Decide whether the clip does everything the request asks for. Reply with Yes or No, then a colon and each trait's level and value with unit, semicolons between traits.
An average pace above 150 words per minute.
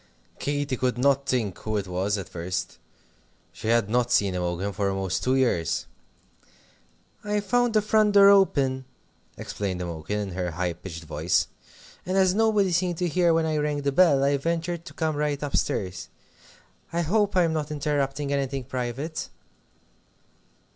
Yes: average, 160 wpm